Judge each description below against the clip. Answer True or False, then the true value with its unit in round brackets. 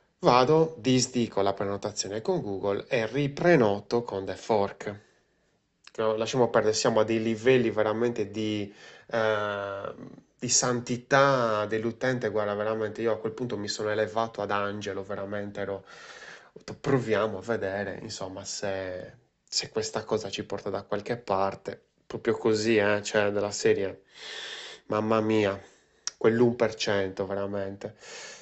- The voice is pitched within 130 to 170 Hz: False (110 Hz)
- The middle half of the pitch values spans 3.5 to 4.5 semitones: False (2.9 semitones)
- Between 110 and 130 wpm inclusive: True (125 wpm)